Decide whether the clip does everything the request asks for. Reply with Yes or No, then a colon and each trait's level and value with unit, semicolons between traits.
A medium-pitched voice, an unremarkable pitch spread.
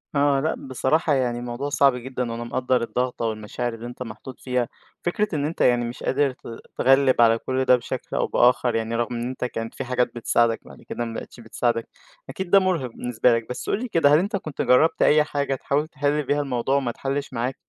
No: low, 125 Hz; average, 3.1 semitones